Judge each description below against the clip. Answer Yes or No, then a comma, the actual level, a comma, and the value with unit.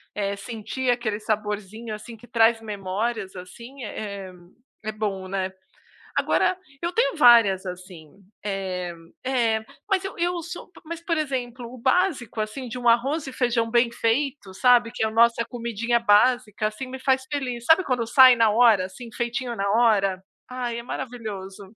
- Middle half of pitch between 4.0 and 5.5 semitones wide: No, average, 3.5 semitones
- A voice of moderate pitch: No, high, 235 Hz